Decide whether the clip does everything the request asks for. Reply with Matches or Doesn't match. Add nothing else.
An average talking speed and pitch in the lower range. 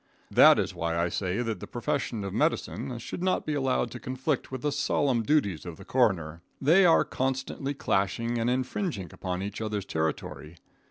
Matches